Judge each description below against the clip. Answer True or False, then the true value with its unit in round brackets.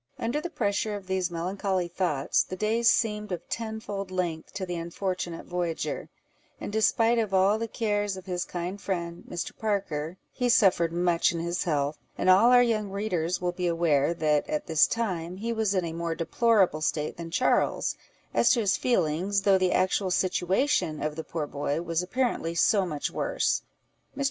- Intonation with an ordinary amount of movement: True (3.7 semitones)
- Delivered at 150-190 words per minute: True (185 wpm)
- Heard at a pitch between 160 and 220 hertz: True (185 Hz)